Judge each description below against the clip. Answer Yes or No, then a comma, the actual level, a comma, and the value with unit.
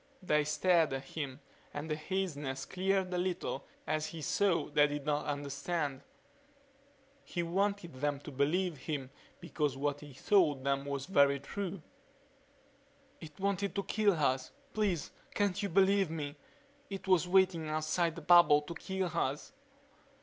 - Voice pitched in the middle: Yes, medium, 155 Hz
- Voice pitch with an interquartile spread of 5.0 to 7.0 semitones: No, average, 4.5 semitones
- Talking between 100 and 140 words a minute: No, average, 150 wpm